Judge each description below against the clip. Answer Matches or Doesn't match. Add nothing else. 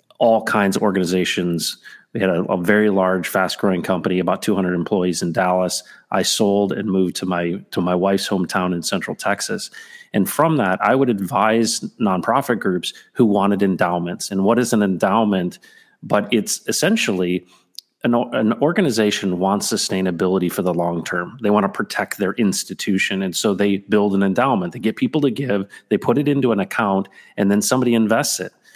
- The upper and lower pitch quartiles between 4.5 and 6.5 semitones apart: Doesn't match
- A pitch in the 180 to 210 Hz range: Doesn't match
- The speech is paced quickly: Doesn't match